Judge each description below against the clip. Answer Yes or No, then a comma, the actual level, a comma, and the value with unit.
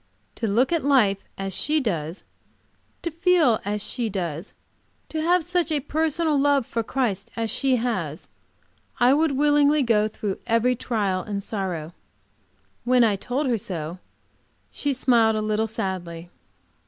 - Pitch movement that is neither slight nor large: No, wide, 6.4 semitones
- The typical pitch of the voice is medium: No, high, 230 Hz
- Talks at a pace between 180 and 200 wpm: No, average, 150 wpm